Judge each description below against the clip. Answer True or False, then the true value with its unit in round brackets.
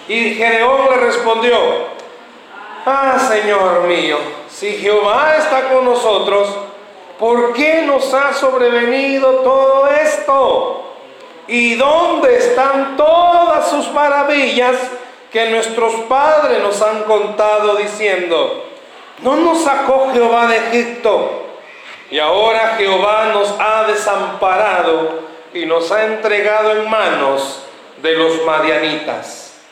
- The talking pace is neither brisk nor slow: False (105 wpm)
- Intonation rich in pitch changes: False (5.0 semitones)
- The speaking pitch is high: True (235 Hz)